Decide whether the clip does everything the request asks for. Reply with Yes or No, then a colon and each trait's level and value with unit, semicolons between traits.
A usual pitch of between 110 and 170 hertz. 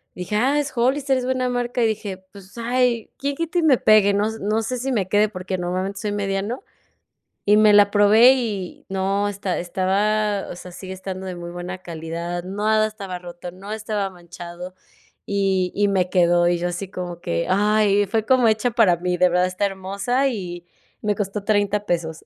No: high, 200 Hz